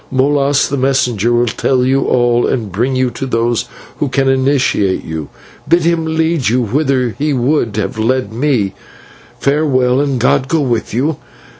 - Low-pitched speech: Yes, low, 130 Hz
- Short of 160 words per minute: No, average, 165 wpm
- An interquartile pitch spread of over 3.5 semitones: No, average, 2.9 semitones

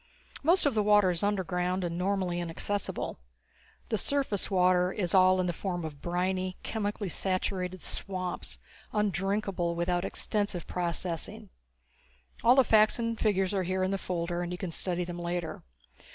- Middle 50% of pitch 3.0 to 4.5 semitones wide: No, narrow, 2.5 semitones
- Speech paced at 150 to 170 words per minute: Yes, average, 155 wpm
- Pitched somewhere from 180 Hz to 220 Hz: Yes, medium, 185 Hz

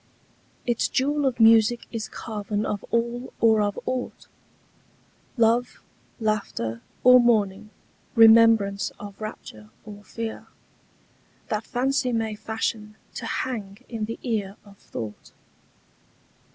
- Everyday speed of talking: No, slow, 110 wpm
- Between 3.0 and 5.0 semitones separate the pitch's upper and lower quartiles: No, narrow, 2.4 semitones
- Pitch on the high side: Yes, high, 220 Hz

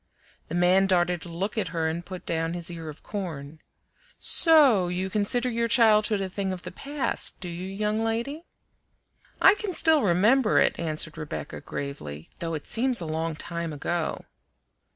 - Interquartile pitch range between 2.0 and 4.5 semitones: No, average, 5.3 semitones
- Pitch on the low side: No, medium, 185 Hz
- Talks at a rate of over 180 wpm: No, average, 175 wpm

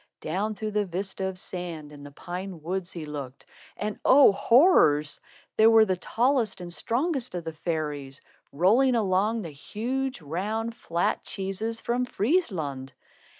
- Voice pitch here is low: No, high, 190 Hz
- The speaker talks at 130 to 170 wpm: Yes, average, 150 wpm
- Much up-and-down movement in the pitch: Yes, wide, 5.8 semitones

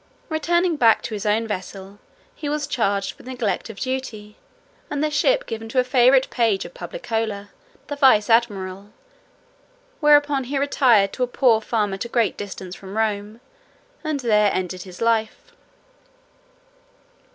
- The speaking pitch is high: Yes, high, 230 Hz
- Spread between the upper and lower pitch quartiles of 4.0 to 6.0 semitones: Yes, average, 4.8 semitones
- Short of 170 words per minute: Yes, average, 150 wpm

